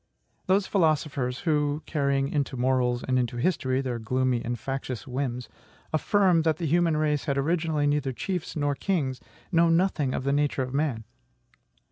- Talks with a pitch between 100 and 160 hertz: Yes, medium, 140 Hz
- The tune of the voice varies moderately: Yes, average, 3.8 semitones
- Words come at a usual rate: Yes, average, 160 wpm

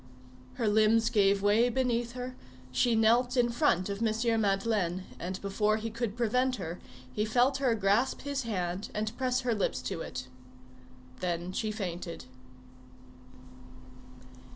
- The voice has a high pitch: Yes, high, 220 Hz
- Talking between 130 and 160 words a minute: Yes, average, 140 wpm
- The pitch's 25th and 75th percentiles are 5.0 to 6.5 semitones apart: No, average, 3.6 semitones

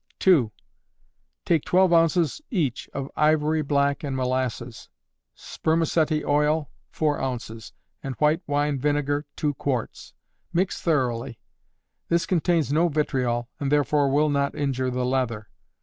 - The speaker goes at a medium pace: No, slow, 125 wpm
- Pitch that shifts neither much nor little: Yes, average, 3.2 semitones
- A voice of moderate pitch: Yes, medium, 145 Hz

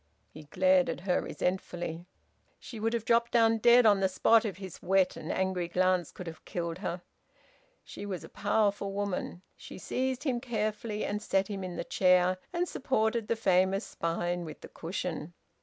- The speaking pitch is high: Yes, high, 195 Hz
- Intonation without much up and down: No, average, 3.6 semitones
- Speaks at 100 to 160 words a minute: No, average, 180 wpm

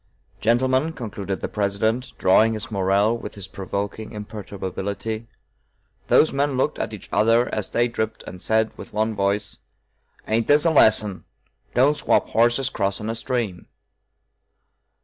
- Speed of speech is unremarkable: Yes, average, 145 wpm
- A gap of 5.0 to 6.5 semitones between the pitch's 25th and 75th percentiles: No, average, 3.0 semitones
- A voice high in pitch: No, low, 110 Hz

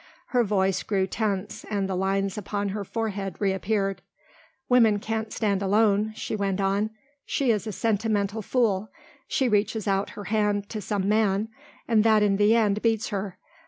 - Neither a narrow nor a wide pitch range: No, narrow, 1.8 semitones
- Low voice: No, high, 205 Hz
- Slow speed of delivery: No, average, 165 wpm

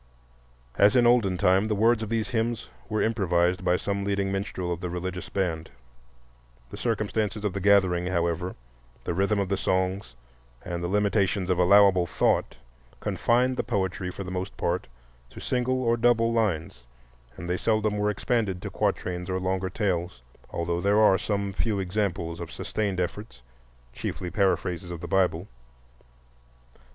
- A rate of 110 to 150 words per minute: No, average, 160 wpm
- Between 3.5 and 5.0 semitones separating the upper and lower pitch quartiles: No, average, 3.0 semitones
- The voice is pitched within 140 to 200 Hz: No, very low, 95 Hz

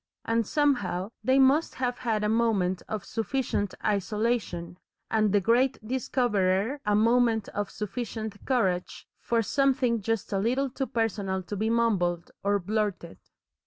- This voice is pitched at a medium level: No, high, 220 Hz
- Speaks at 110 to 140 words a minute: Yes, slow, 135 wpm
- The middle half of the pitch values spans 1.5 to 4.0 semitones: Yes, average, 3.5 semitones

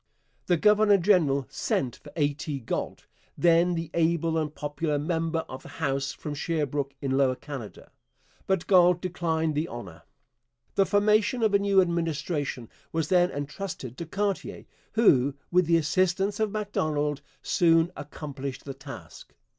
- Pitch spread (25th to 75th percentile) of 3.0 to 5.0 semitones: Yes, average, 4.0 semitones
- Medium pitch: Yes, medium, 160 Hz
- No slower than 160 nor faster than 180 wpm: No, average, 145 wpm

